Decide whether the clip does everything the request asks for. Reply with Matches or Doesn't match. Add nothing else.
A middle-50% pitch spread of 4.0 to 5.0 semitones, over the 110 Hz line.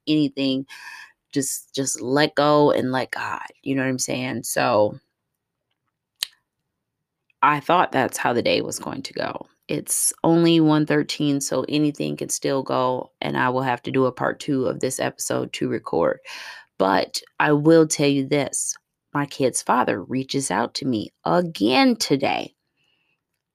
Doesn't match